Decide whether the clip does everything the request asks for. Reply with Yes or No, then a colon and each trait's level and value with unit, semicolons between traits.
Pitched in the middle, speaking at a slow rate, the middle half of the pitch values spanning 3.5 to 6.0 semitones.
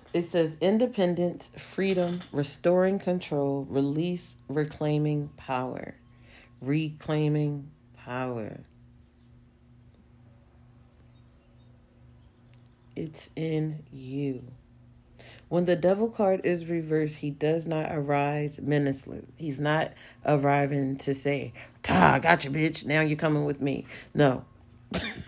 Yes: medium, 145 Hz; slow, 95 wpm; average, 4.2 semitones